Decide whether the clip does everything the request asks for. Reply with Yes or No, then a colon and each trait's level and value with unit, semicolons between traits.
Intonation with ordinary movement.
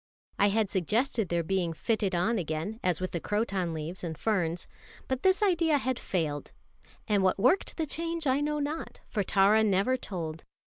No: wide, 6.7 semitones